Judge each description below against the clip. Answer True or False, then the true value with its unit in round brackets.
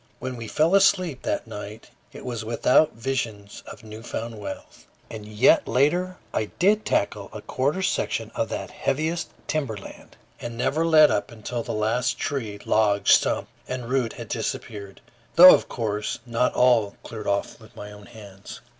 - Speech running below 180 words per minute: True (170 wpm)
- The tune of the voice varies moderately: True (4.4 semitones)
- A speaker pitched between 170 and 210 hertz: False (115 Hz)